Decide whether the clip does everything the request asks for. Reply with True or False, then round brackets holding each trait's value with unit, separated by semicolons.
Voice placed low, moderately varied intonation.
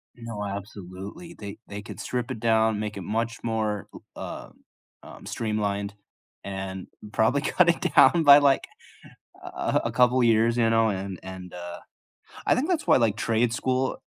True (110 Hz; 3.4 semitones)